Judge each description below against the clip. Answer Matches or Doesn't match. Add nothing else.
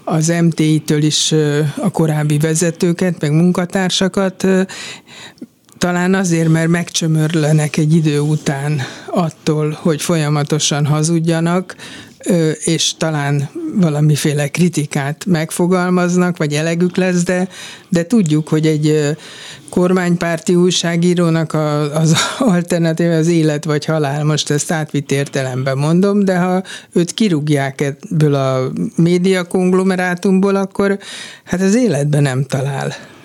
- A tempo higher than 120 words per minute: Doesn't match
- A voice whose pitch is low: Doesn't match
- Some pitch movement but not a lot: Matches